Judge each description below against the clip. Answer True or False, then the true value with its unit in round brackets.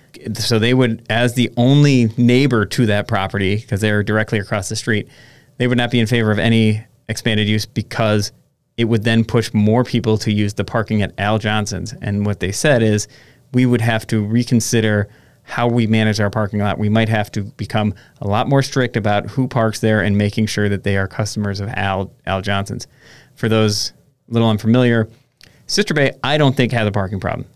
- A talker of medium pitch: False (110 Hz)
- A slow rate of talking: False (205 wpm)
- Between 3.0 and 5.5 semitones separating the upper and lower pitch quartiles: False (2.5 semitones)